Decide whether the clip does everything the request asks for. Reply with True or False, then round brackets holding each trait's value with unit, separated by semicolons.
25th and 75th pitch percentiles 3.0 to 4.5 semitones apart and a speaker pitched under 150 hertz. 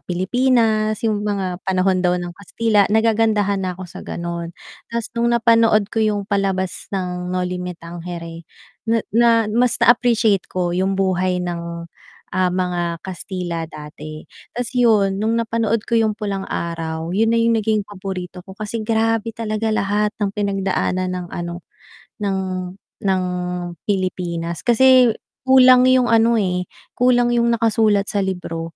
False (3.9 semitones; 200 Hz)